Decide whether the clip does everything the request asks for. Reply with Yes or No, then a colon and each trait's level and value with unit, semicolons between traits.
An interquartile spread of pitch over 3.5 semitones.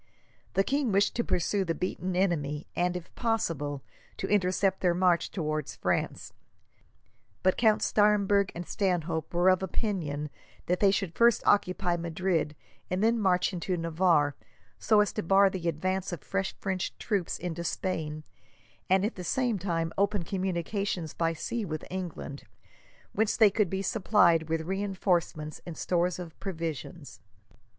No: average, 3.0 semitones